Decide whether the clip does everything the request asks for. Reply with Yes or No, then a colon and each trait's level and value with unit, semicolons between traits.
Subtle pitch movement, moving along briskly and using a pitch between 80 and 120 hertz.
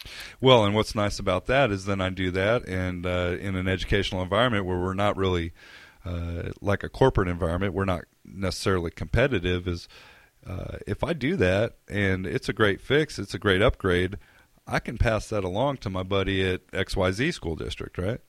No: narrow, 2.1 semitones; average, 190 wpm; very low, 95 Hz